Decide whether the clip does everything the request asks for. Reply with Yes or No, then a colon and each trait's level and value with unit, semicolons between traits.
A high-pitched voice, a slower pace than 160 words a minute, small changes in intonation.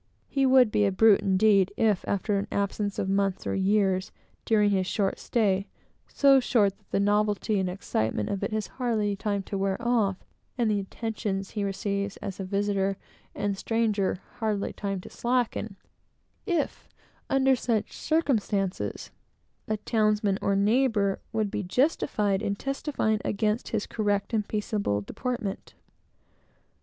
Yes: high, 205 Hz; average, 150 wpm; narrow, 2.2 semitones